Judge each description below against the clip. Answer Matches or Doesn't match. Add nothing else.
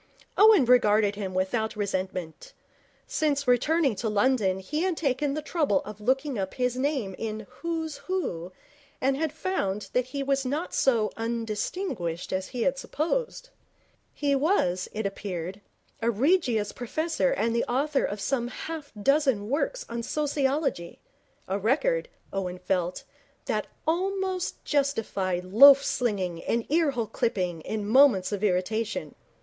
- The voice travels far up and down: Matches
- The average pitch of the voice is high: Matches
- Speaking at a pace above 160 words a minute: Doesn't match